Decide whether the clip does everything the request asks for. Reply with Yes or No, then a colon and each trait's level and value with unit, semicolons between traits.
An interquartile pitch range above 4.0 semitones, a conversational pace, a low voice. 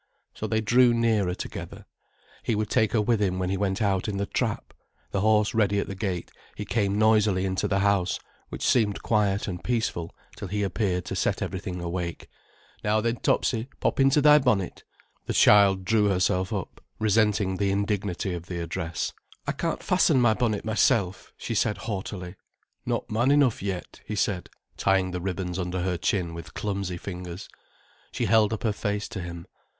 No: average, 2.9 semitones; average, 185 wpm; low, 100 Hz